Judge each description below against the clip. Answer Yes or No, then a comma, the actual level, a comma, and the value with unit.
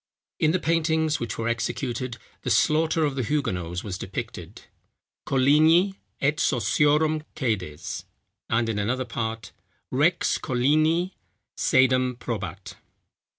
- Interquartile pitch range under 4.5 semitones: No, average, 5.3 semitones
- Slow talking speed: Yes, slow, 110 wpm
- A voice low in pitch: Yes, low, 130 Hz